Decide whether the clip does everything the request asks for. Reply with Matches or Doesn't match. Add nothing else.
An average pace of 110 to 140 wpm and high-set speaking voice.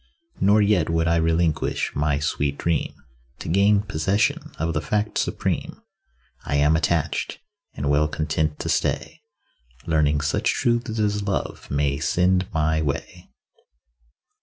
Doesn't match